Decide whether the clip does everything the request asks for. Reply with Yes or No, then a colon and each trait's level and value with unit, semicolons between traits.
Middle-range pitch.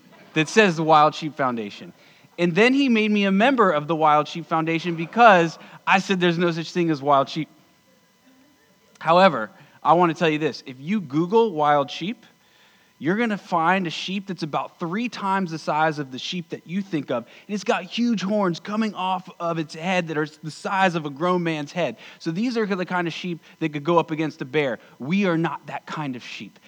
Yes: medium, 175 Hz